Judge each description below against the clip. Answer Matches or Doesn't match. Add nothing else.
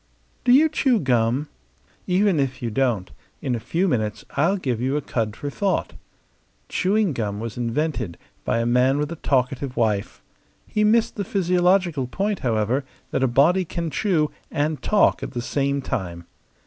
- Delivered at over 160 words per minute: Matches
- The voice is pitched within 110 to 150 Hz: Matches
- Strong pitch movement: Matches